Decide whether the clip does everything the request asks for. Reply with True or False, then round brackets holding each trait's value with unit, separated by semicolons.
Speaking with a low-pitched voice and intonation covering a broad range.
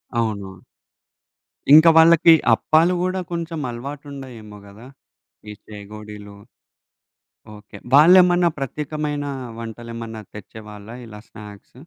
True (120 Hz; 6.8 semitones)